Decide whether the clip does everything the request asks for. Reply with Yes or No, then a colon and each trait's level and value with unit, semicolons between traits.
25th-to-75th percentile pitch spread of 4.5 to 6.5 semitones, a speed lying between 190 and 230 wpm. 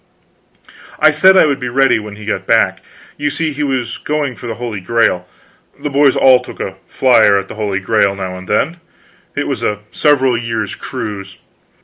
Yes: wide, 5.5 semitones; average, 195 wpm